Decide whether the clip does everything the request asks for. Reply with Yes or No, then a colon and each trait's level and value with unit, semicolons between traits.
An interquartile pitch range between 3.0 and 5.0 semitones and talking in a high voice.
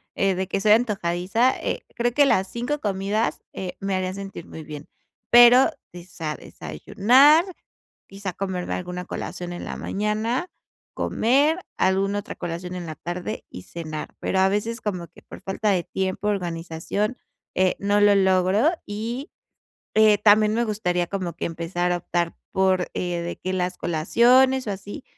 Yes: average, 3.4 semitones; high, 195 Hz